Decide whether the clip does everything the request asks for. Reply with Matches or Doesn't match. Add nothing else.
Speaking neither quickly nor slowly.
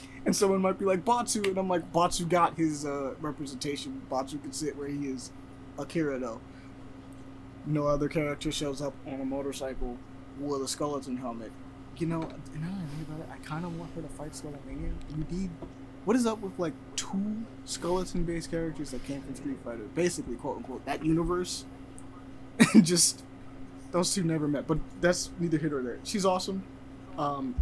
Matches